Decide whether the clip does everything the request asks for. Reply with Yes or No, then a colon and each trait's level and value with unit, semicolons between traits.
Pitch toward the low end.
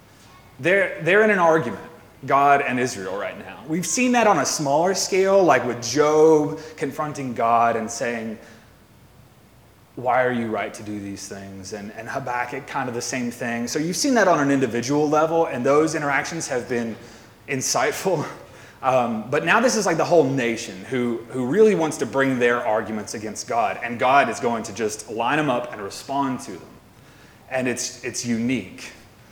Yes: low, 125 Hz